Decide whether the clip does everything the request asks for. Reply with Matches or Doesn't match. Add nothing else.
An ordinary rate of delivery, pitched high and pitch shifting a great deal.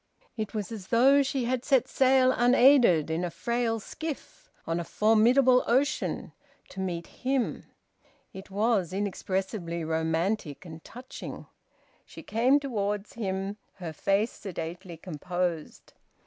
Doesn't match